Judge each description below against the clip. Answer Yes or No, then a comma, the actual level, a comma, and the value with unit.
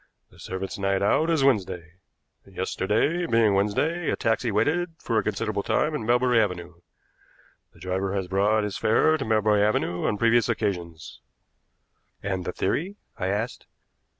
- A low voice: Yes, low, 105 Hz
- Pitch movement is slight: No, average, 4.0 semitones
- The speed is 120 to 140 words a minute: No, average, 150 wpm